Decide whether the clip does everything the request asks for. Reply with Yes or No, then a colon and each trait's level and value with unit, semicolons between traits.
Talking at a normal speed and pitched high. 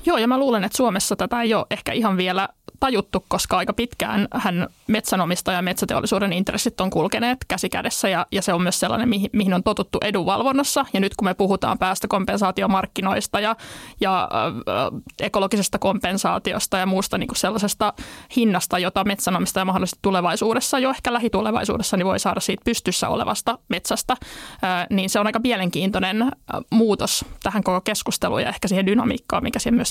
No: fast, 170 wpm; high, 205 Hz